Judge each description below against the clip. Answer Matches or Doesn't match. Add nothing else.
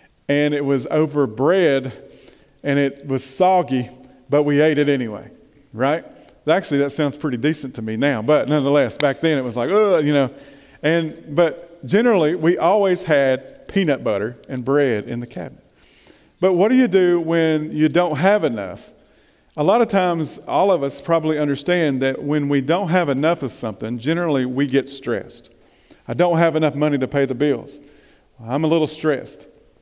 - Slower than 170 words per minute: Doesn't match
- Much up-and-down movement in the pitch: Doesn't match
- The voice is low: Doesn't match